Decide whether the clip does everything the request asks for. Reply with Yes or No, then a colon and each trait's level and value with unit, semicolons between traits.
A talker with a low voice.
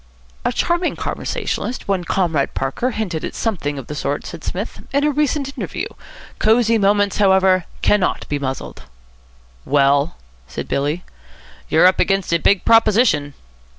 No: high, 190 Hz